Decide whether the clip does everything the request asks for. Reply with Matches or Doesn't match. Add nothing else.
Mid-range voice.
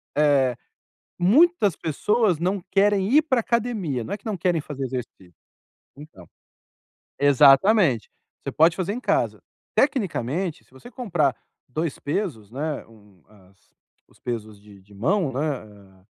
Matches